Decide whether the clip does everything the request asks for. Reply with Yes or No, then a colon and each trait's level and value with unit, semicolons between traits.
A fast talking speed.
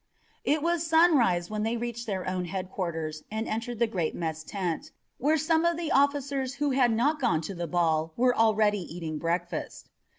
No: average, 185 wpm